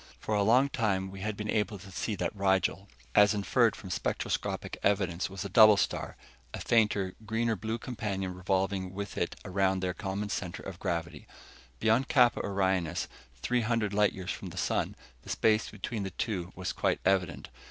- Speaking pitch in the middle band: No, low, 100 Hz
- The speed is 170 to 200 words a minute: Yes, average, 180 wpm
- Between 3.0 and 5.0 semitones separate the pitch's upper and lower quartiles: No, narrow, 2.4 semitones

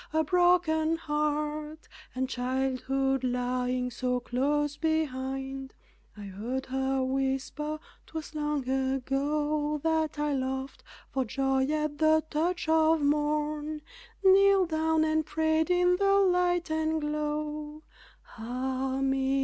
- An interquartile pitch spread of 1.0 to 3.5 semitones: Yes, average, 3.0 semitones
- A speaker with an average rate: No, slow, 115 wpm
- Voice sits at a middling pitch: No, very high, 295 Hz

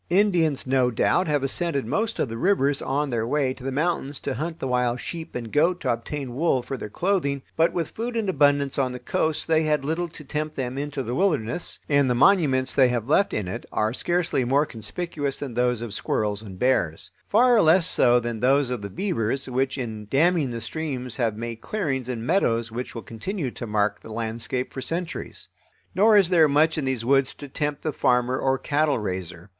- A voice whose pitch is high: No, low, 135 Hz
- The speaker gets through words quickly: Yes, fast, 210 wpm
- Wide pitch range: No, average, 4.9 semitones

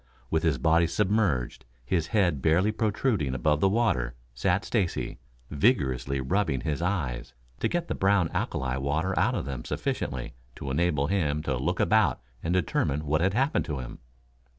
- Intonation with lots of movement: Yes, wide, 6.1 semitones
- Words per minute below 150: No, average, 165 wpm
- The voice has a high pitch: No, very low, 80 Hz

